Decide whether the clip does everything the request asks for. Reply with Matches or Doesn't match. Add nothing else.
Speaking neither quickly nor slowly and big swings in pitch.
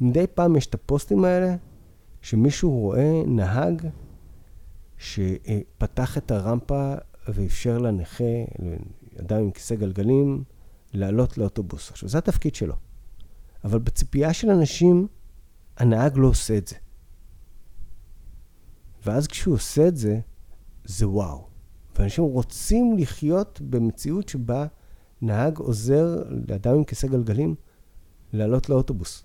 Matches